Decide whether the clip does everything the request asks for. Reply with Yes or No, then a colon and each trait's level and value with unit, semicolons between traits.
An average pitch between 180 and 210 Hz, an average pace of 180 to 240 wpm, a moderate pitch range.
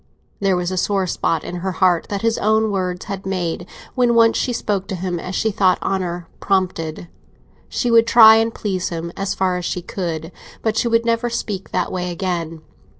Yes: high, 190 Hz; fast, 205 wpm; average, 3.5 semitones